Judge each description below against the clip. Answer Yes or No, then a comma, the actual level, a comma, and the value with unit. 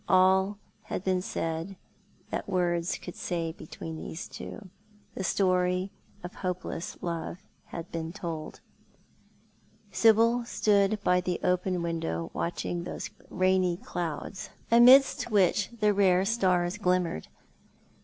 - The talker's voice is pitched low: No, medium, 180 Hz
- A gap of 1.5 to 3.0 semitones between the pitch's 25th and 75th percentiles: Yes, narrow, 2.5 semitones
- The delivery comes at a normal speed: No, slow, 115 wpm